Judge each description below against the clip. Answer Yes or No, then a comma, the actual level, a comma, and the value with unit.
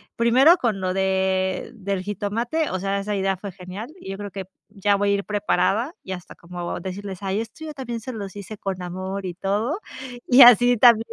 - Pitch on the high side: Yes, high, 200 Hz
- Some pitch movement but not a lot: Yes, average, 3.3 semitones